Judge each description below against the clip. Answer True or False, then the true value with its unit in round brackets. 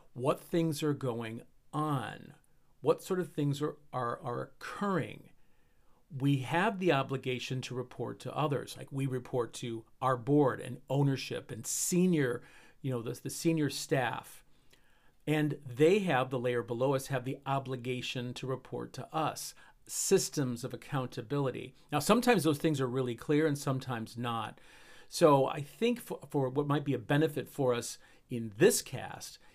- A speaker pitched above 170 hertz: False (135 Hz)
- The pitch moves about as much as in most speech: True (3.0 semitones)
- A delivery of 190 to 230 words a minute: False (160 wpm)